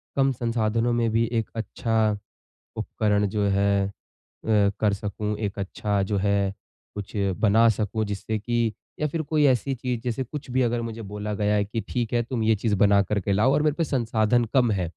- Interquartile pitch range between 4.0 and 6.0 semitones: No, average, 2.7 semitones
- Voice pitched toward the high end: No, low, 110 Hz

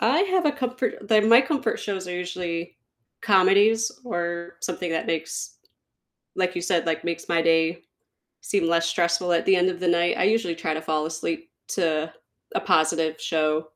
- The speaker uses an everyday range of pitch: Yes, average, 3.9 semitones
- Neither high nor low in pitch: Yes, medium, 175 Hz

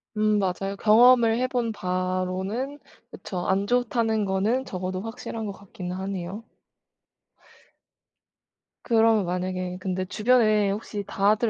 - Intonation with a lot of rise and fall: No, average, 3.4 semitones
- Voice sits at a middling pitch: No, high, 205 Hz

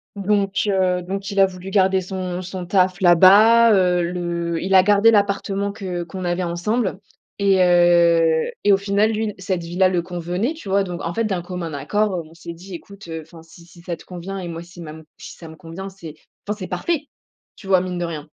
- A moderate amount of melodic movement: No, narrow, 2.3 semitones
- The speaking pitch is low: No, medium, 185 Hz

